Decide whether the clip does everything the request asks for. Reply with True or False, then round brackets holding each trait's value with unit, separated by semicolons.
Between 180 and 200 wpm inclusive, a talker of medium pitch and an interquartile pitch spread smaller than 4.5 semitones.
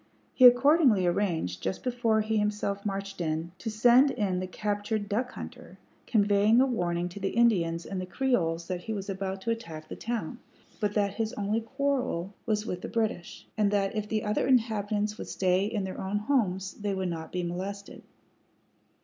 False (185 wpm; 205 Hz; 3.2 semitones)